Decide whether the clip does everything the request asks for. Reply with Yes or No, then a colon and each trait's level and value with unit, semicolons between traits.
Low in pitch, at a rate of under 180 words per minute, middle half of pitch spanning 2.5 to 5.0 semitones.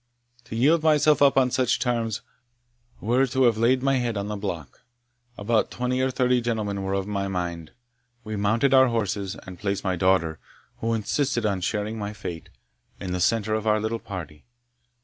No: low, 110 Hz; average, 185 wpm; average, 4.2 semitones